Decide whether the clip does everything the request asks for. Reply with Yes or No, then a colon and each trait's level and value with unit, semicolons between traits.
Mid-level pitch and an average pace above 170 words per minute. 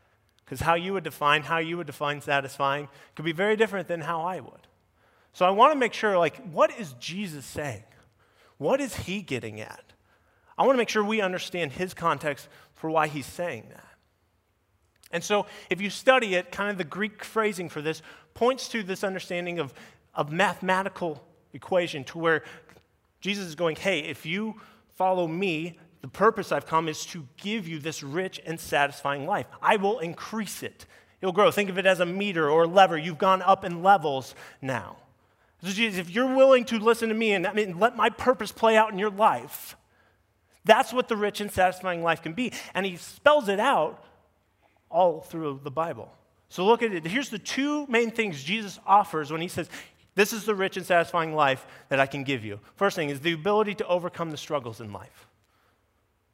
Yes: medium, 180 Hz; average, 200 wpm